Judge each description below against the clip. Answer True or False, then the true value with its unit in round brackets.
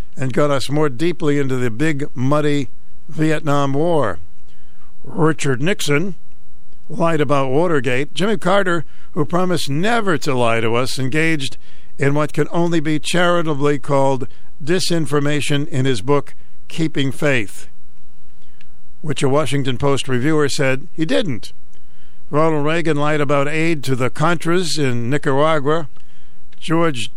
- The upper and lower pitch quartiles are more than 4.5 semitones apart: False (3.6 semitones)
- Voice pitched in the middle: True (145 Hz)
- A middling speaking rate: False (130 wpm)